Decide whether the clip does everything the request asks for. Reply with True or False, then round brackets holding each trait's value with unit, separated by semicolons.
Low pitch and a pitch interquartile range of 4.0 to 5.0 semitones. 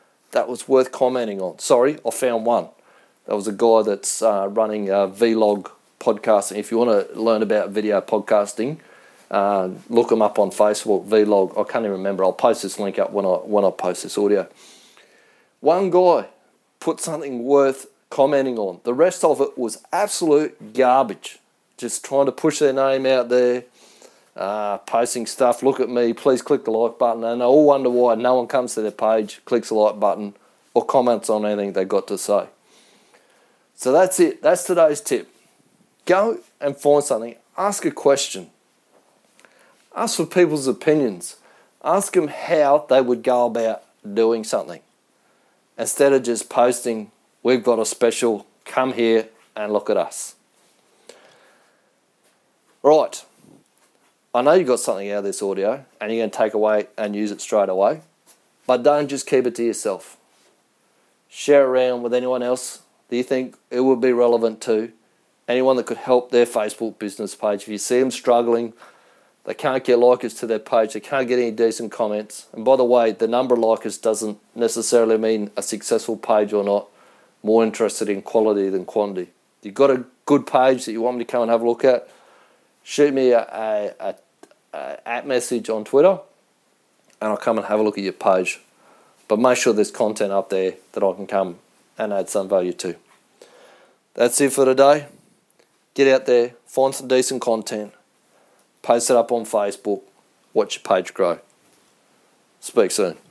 False (120 Hz; 3.4 semitones)